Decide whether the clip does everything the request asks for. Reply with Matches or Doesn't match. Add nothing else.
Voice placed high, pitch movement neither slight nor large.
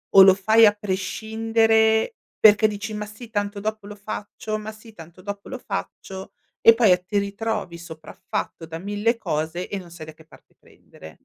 Matches